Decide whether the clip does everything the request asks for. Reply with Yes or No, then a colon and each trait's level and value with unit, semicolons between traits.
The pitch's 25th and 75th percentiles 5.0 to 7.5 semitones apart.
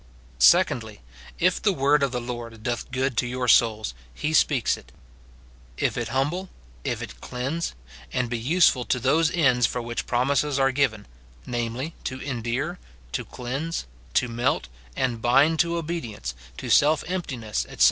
No: average, 4.0 semitones